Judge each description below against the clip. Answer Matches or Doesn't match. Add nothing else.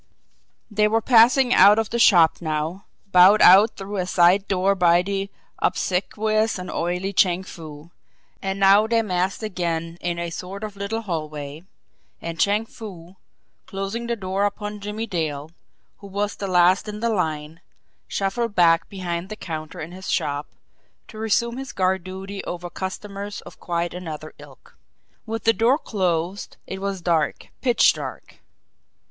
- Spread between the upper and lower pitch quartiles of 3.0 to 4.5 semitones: Matches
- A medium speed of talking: Matches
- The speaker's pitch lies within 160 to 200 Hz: Matches